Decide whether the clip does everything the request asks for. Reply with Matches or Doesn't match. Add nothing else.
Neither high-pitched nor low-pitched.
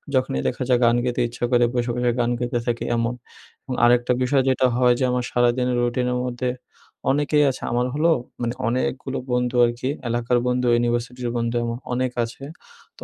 Doesn't match